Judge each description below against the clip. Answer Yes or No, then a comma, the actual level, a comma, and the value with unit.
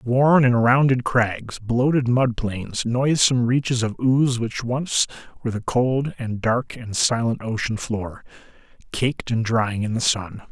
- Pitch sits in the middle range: No, low, 120 Hz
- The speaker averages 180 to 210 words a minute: No, average, 160 wpm